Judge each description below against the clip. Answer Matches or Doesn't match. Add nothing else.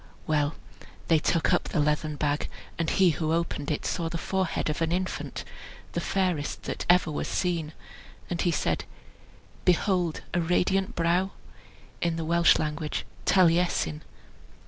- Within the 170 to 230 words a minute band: Doesn't match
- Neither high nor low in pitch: Matches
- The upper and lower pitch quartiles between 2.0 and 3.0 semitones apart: Matches